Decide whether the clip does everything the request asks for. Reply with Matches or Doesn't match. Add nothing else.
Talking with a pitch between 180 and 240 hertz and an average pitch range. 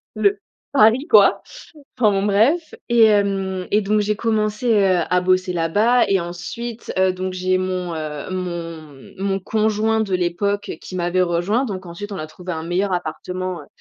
Matches